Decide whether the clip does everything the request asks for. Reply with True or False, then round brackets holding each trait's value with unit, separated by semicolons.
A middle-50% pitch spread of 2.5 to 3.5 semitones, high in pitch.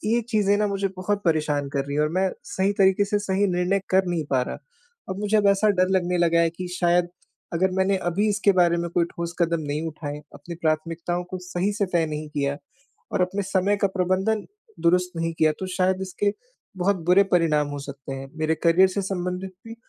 False (2.8 semitones; 180 Hz)